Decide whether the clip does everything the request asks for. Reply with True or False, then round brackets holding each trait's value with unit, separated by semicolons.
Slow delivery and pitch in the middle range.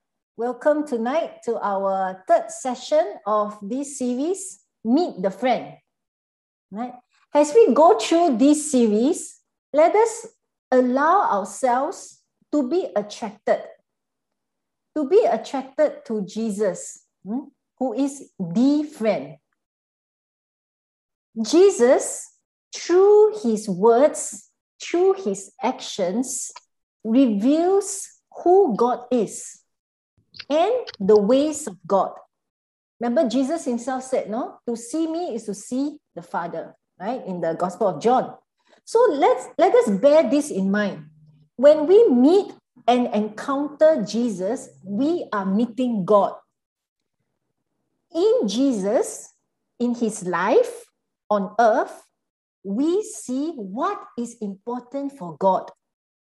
False (110 wpm; 255 Hz)